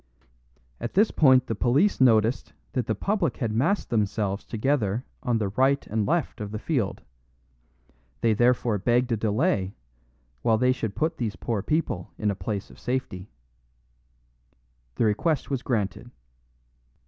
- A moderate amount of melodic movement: Yes, average, 4.0 semitones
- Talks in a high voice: No, low, 120 Hz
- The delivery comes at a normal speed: Yes, average, 150 wpm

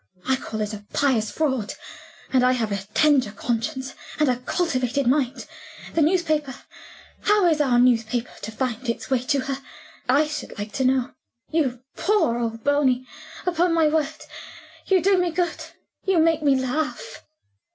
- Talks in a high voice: Yes, very high, 265 Hz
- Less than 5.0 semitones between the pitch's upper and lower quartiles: Yes, average, 4.4 semitones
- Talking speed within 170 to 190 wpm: No, average, 160 wpm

